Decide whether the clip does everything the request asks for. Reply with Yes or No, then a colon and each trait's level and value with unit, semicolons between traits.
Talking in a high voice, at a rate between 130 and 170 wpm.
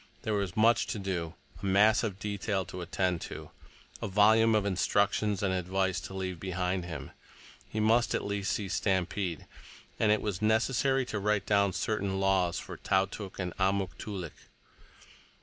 No: low, 100 Hz; average, 165 wpm